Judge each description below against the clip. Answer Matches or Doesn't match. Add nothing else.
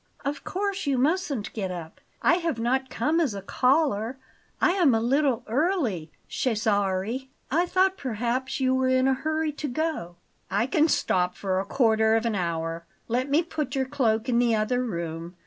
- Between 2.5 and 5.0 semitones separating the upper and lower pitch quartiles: Doesn't match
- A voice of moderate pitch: Doesn't match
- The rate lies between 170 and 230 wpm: Matches